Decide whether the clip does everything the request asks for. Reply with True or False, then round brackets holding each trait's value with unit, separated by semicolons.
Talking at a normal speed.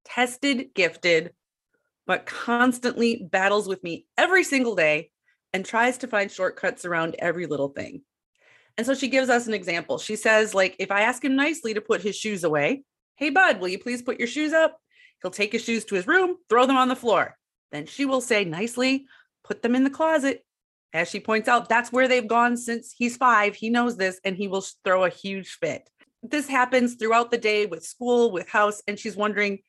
False (210 wpm)